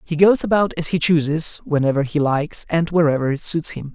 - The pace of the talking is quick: Yes, fast, 215 wpm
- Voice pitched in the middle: Yes, medium, 155 Hz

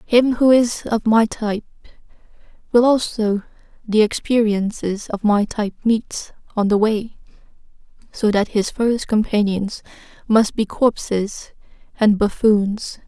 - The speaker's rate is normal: No, slow, 125 wpm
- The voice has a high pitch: Yes, high, 215 Hz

